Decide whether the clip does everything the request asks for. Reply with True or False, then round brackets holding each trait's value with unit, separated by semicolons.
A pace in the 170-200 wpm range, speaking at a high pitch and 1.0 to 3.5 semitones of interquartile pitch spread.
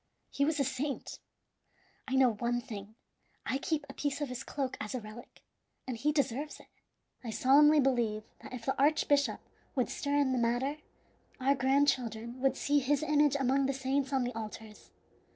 True (180 wpm; 265 Hz; 2.8 semitones)